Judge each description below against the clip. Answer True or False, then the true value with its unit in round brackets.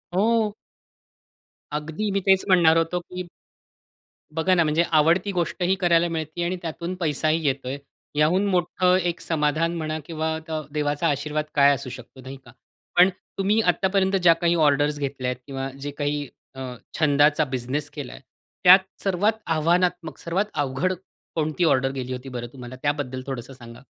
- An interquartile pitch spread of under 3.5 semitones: False (3.8 semitones)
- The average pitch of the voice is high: False (155 Hz)